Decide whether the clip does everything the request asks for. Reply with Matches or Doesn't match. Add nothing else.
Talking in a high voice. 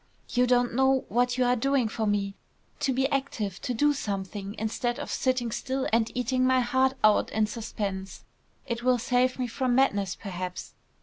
Matches